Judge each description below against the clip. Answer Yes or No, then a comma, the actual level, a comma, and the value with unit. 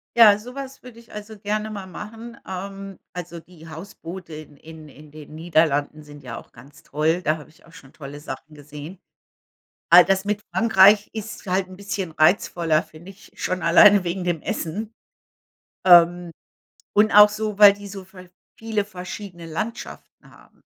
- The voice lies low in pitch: No, medium, 185 Hz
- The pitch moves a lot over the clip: No, average, 4.5 semitones